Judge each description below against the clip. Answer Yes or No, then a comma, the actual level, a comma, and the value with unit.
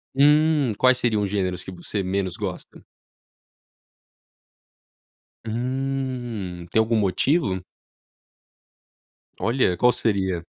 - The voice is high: No, low, 110 Hz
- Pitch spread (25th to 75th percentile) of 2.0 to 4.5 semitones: No, wide, 5.5 semitones